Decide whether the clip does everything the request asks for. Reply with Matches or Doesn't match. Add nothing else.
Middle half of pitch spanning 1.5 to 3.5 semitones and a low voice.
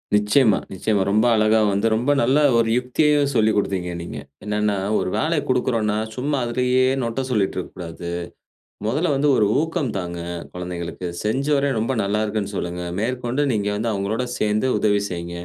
Doesn't match